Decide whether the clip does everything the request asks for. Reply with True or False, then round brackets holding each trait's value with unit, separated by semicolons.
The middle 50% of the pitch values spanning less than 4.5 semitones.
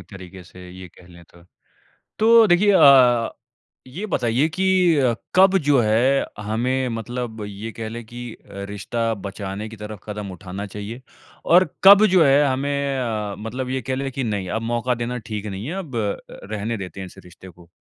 False (4.9 semitones)